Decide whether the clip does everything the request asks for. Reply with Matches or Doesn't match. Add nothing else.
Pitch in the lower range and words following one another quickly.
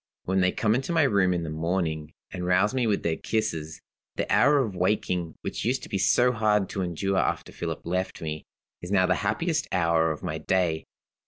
Matches